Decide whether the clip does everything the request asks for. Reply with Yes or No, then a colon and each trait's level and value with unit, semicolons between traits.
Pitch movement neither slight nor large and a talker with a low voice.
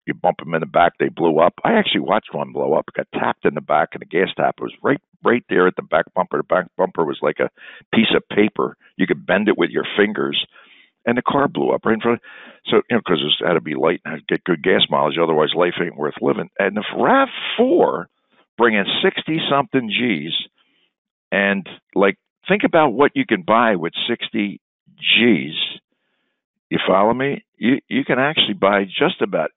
No: wide, 6.2 semitones; low, 105 Hz